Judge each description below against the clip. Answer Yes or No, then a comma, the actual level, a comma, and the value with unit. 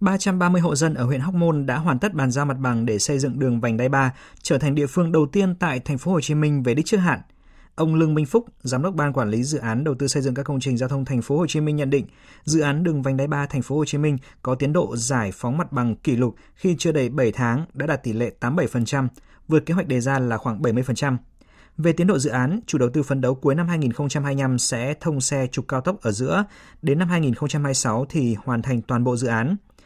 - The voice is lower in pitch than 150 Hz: Yes, medium, 140 Hz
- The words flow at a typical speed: No, fast, 265 wpm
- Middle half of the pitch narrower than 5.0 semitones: Yes, average, 3.9 semitones